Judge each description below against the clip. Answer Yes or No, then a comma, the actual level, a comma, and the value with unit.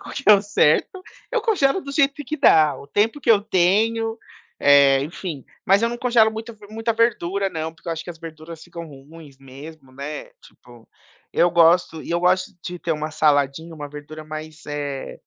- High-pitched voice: No, medium, 170 Hz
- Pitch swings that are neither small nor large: No, wide, 6.5 semitones